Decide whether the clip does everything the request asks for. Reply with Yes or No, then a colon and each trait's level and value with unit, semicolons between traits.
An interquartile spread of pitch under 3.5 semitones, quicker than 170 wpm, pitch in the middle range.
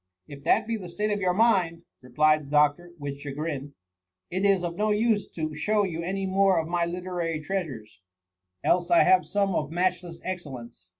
No: average, 4.3 semitones; average, 200 wpm; medium, 175 Hz